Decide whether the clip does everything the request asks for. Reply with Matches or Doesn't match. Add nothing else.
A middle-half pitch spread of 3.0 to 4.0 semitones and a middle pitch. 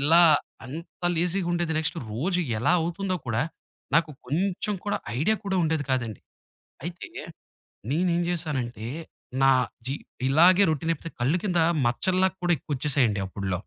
Doesn't match